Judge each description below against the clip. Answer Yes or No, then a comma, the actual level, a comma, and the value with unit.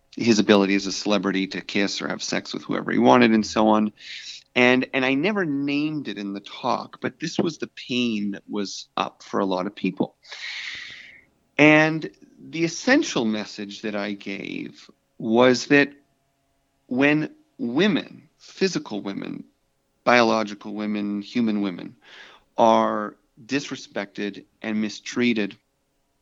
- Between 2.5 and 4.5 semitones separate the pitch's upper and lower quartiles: No, average, 5.1 semitones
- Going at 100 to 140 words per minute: Yes, slow, 135 wpm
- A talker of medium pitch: No, low, 115 Hz